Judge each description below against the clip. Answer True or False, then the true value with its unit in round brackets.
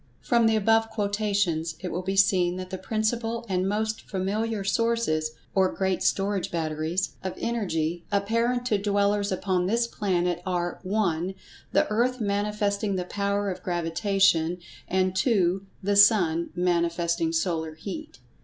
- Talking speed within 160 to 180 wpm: False (140 wpm)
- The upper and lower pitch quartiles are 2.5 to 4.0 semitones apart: True (3.3 semitones)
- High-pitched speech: True (195 Hz)